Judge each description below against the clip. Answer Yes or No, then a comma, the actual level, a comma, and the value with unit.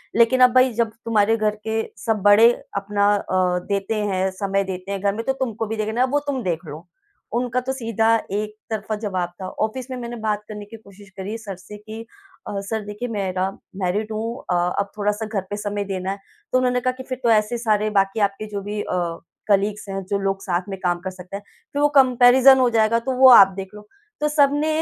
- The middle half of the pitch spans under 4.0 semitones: Yes, average, 3.0 semitones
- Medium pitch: No, high, 210 Hz